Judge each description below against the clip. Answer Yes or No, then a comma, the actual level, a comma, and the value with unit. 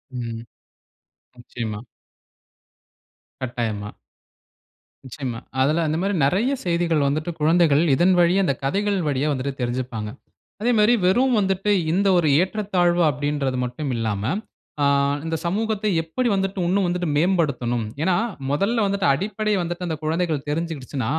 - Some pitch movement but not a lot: No, wide, 6.3 semitones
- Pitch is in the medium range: Yes, medium, 165 Hz